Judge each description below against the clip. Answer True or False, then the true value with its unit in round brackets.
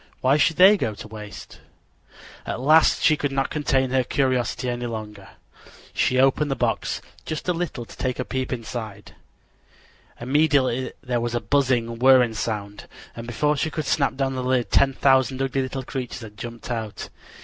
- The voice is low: True (130 Hz)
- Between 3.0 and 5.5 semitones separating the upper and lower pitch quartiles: False (2.6 semitones)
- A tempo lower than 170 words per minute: False (175 wpm)